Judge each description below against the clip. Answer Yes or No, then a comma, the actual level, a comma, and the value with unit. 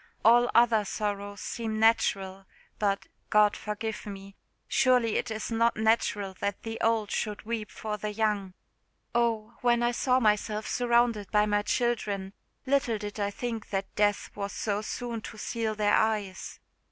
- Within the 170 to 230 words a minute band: No, average, 155 wpm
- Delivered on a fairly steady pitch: Yes, narrow, 2.1 semitones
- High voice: Yes, high, 215 Hz